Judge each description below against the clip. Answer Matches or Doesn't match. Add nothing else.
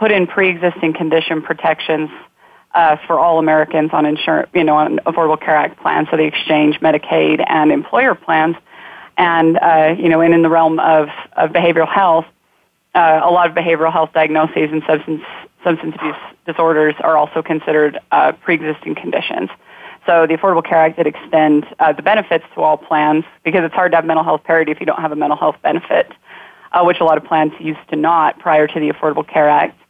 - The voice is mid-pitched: Matches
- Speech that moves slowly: Doesn't match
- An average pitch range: Doesn't match